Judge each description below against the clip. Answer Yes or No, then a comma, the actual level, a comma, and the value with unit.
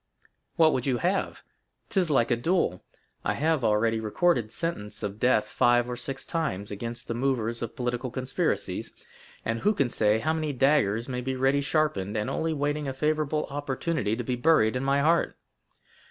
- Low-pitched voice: Yes, low, 130 Hz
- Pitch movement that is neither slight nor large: Yes, average, 4.9 semitones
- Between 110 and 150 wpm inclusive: No, average, 180 wpm